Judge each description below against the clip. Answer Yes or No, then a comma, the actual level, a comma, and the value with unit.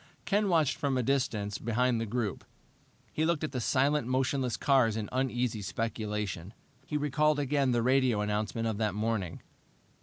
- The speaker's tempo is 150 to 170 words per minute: Yes, average, 160 wpm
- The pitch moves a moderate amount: Yes, average, 4.1 semitones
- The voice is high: No, low, 125 Hz